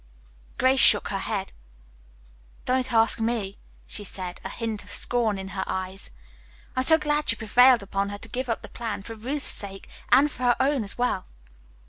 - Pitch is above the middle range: Yes, high, 225 Hz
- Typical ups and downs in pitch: Yes, average, 4.3 semitones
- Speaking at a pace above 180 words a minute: Yes, average, 190 wpm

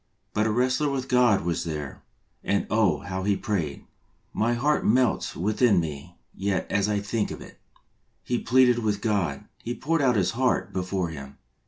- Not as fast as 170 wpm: No, average, 175 wpm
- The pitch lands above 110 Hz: No, low, 105 Hz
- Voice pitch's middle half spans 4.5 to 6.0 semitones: Yes, average, 5.1 semitones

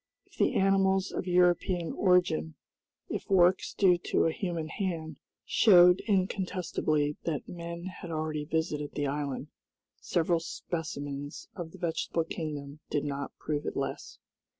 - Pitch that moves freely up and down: No, average, 3.3 semitones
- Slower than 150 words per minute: Yes, slow, 135 wpm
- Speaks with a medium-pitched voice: Yes, medium, 165 Hz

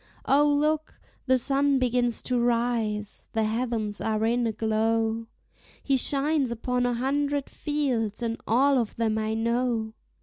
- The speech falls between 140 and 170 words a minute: Yes, average, 145 wpm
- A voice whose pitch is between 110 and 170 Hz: No, high, 240 Hz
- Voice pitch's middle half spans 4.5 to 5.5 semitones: No, average, 3.4 semitones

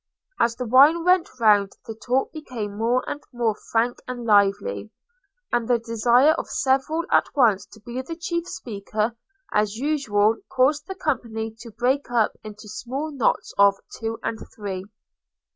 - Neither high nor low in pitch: No, high, 235 Hz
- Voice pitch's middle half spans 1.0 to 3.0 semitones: No, average, 3.8 semitones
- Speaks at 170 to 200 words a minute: No, average, 160 wpm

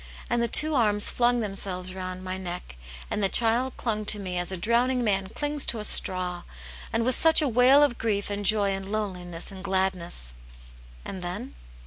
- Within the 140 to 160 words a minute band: No, average, 190 wpm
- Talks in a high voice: Yes, high, 205 Hz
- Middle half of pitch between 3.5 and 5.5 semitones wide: Yes, average, 4.3 semitones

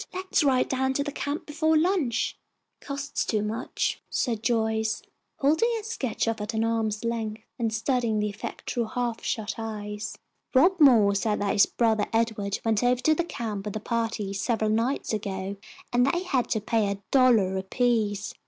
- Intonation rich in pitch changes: No, average, 3.5 semitones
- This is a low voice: No, high, 225 Hz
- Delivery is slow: No, average, 175 wpm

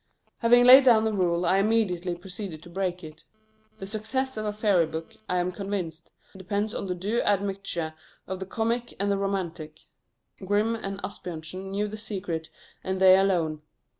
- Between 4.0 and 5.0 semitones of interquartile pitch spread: No, average, 3.2 semitones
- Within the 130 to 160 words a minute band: No, average, 170 wpm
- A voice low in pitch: No, high, 195 Hz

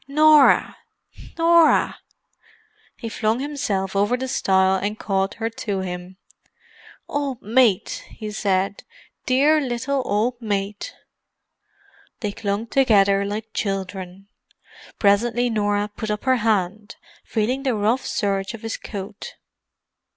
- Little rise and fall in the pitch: No, average, 4.1 semitones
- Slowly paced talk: Yes, slow, 115 wpm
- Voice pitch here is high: Yes, high, 215 Hz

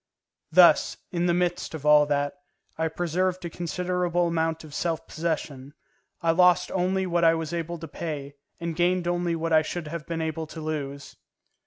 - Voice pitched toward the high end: No, medium, 165 Hz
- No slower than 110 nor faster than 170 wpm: No, average, 180 wpm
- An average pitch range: No, narrow, 1.9 semitones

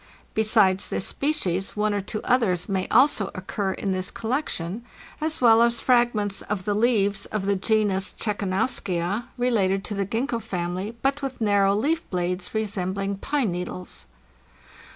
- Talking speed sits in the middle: Yes, average, 150 wpm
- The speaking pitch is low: No, high, 205 Hz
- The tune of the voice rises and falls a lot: No, average, 3.6 semitones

